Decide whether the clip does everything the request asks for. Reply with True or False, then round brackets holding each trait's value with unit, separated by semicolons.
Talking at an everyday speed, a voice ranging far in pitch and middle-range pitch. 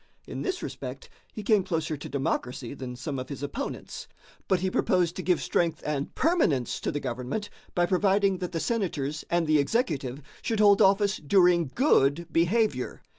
True (175 wpm; 6.1 semitones; 175 Hz)